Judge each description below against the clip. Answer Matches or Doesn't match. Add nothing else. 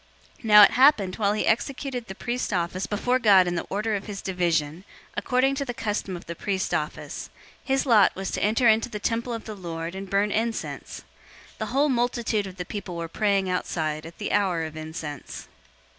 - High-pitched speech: Matches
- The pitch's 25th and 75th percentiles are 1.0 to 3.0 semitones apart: Doesn't match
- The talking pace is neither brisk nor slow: Doesn't match